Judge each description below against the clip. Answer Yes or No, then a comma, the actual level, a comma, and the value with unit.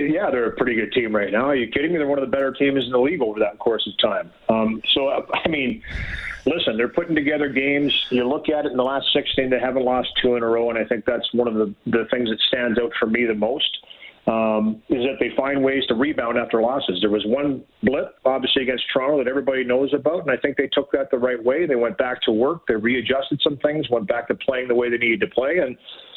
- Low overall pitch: Yes, low, 130 Hz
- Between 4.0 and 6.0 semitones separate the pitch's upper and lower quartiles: No, average, 2.9 semitones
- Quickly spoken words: Yes, fast, 265 wpm